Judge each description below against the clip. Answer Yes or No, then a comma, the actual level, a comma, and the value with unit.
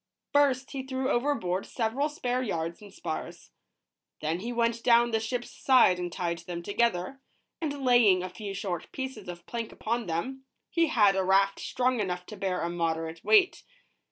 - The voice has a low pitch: No, high, 220 Hz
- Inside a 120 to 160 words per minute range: No, average, 175 wpm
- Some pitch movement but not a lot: No, wide, 6.1 semitones